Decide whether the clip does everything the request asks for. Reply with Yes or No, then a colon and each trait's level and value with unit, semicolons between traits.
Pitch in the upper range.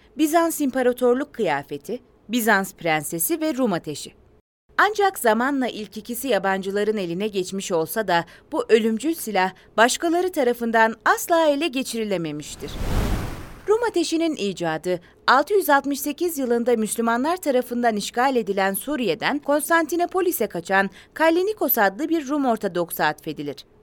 Yes: high, 235 Hz